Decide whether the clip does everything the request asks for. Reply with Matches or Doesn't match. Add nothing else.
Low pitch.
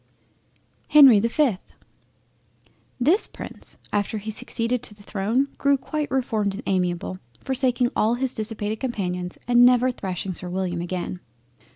Doesn't match